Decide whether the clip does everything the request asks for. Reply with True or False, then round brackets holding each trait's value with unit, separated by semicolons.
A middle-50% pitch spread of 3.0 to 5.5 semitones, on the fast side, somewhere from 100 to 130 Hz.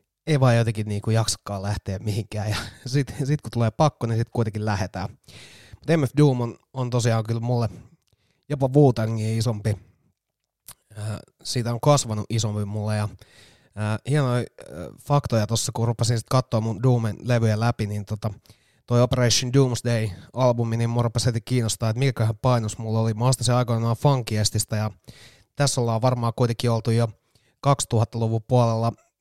False (2.5 semitones; 160 wpm; 115 Hz)